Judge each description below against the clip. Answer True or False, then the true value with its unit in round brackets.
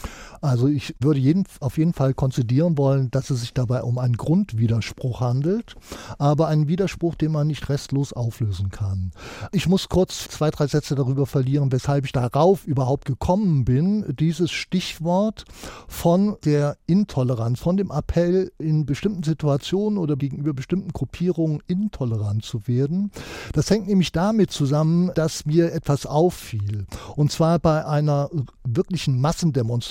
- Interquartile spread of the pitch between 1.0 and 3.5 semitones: False (4.5 semitones)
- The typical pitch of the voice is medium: True (150 Hz)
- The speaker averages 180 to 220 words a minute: False (145 wpm)